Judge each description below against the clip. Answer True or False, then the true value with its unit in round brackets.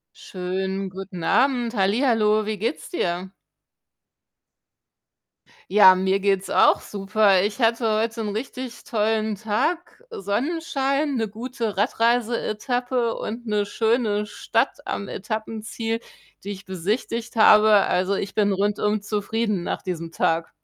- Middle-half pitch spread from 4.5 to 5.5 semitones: False (2.9 semitones)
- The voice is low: False (215 Hz)